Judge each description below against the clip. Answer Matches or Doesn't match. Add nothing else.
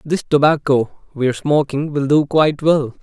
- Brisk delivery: Doesn't match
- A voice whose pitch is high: Doesn't match